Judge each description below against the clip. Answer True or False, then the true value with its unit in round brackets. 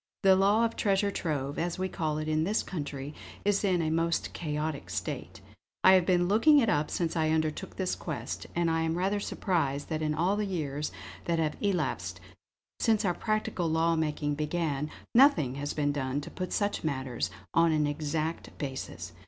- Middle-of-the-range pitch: True (160 Hz)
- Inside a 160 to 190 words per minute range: True (185 wpm)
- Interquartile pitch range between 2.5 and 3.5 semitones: False (4.1 semitones)